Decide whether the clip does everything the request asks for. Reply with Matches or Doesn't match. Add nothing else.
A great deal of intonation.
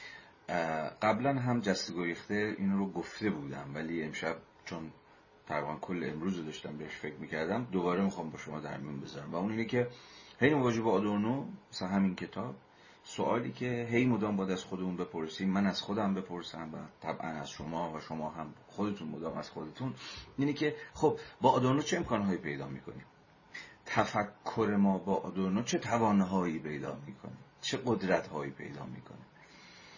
Matches